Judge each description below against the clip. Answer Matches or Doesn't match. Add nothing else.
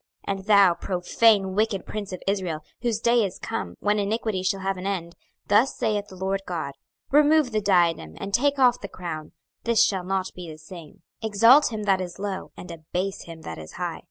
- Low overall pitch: Doesn't match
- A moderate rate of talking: Doesn't match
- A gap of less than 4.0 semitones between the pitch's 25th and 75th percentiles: Matches